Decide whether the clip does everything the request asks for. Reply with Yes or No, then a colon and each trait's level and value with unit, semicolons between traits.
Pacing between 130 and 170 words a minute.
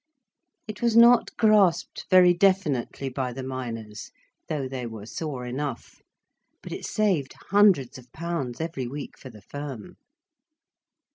Yes: slow, 135 wpm